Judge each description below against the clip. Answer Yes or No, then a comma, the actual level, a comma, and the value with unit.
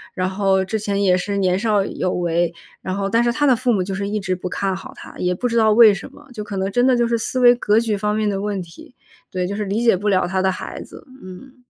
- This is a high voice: Yes, high, 200 Hz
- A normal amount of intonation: Yes, average, 3.4 semitones